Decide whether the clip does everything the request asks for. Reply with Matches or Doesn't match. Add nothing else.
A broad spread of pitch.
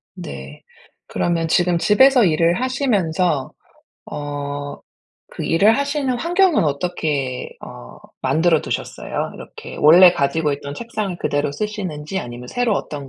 Matches